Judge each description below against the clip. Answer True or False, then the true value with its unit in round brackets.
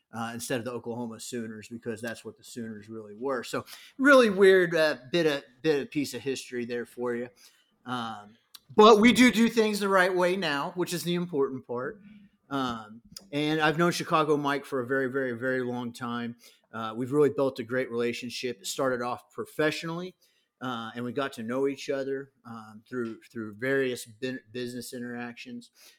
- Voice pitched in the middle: False (130 Hz)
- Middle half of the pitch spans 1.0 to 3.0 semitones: False (5.0 semitones)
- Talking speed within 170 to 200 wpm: True (185 wpm)